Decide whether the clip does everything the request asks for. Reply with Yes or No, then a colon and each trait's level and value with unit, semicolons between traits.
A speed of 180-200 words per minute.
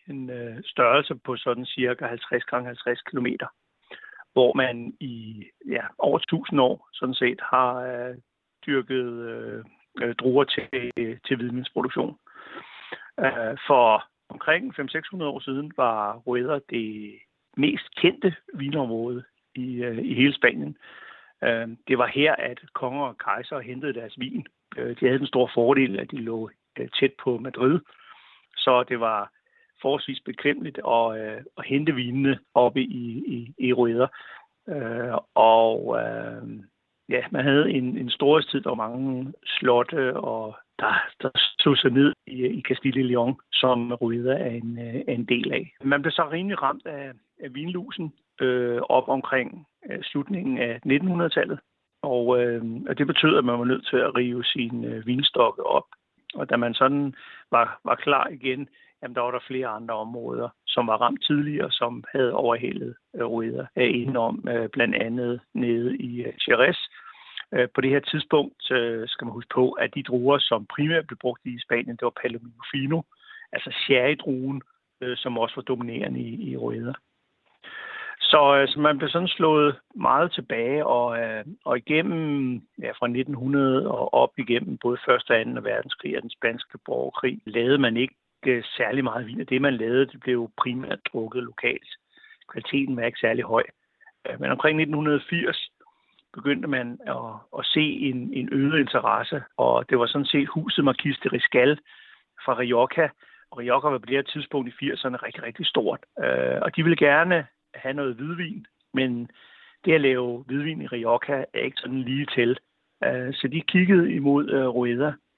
No: average, 165 wpm